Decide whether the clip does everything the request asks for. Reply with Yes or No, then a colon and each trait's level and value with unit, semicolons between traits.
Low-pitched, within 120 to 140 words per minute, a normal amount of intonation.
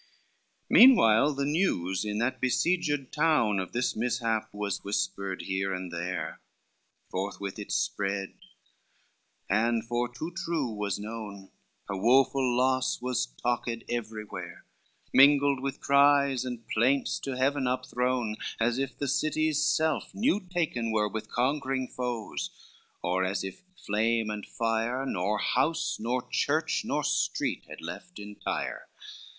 Yes: low, 120 Hz; slow, 135 wpm; average, 4.7 semitones